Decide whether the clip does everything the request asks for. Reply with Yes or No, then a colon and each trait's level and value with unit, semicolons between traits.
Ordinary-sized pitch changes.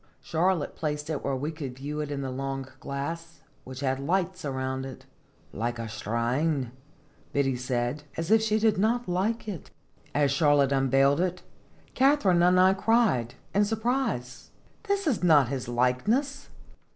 No: wide, 6.3 semitones